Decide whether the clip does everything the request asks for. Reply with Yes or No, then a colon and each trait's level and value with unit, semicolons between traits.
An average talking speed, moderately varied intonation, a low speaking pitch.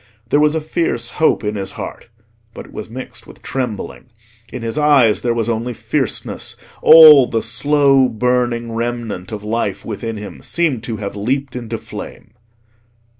Yes: average, 165 wpm; average, 3.5 semitones; low, 120 Hz